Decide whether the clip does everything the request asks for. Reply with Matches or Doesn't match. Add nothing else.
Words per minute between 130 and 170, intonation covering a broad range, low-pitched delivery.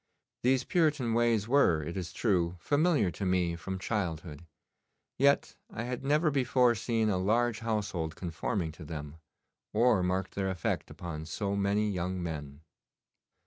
Matches